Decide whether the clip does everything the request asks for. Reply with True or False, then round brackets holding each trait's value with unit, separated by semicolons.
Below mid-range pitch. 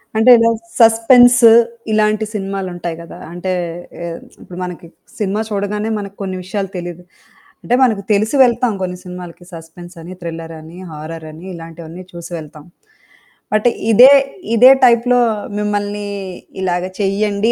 False (195 Hz)